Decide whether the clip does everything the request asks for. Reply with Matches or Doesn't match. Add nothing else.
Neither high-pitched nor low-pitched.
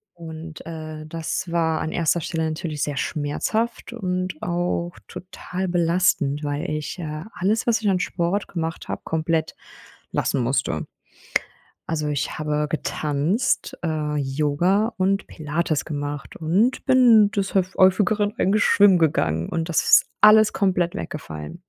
Matches